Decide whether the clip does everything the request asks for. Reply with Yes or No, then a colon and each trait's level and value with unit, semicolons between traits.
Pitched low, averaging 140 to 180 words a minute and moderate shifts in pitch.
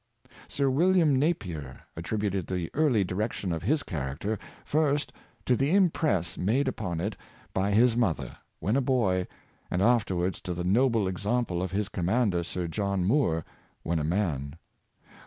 No: low, 100 Hz; average, 155 wpm; wide, 6.2 semitones